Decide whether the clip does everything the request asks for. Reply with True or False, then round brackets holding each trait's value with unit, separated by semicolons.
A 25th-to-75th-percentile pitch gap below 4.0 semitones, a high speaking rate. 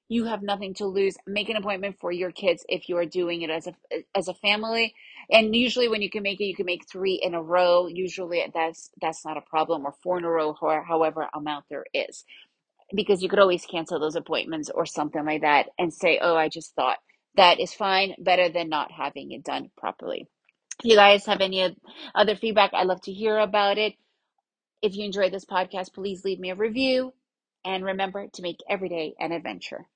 True (3.4 semitones; 220 wpm)